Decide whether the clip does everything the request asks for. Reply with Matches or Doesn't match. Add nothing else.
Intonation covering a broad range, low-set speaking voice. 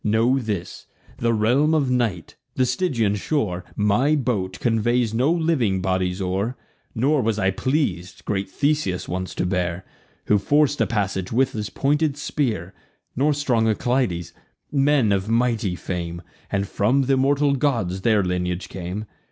Matches